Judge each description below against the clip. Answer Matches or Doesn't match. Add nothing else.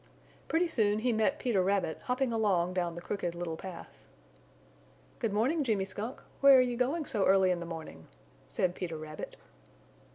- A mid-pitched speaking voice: Doesn't match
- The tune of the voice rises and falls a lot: Matches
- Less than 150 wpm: Doesn't match